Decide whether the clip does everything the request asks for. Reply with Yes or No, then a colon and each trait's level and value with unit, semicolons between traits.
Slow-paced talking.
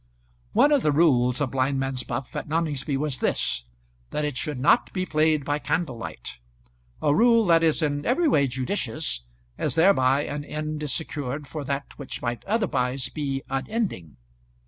No: average, 170 wpm